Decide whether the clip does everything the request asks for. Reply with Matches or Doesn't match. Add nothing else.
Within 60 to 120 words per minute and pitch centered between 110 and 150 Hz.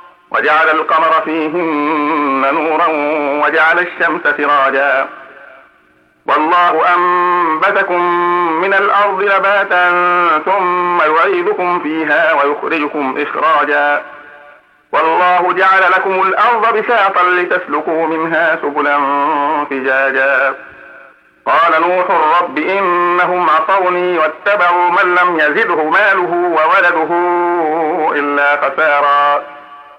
Doesn't match